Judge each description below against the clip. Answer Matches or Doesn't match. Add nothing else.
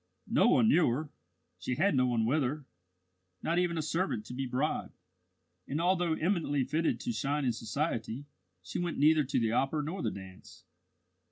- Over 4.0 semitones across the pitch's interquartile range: Matches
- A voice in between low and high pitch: Matches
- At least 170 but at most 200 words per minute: Matches